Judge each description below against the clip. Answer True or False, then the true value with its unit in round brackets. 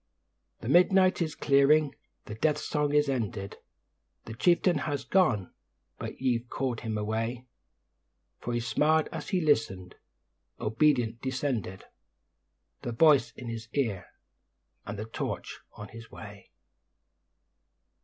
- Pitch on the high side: False (125 Hz)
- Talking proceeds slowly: True (125 wpm)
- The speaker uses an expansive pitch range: False (5.0 semitones)